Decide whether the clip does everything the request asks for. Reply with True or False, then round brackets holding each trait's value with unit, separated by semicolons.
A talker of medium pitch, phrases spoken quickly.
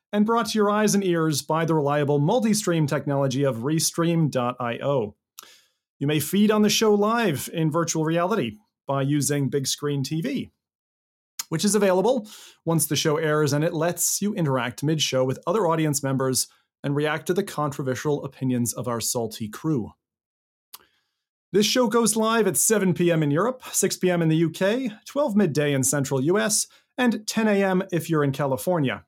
False (160 Hz; 175 wpm)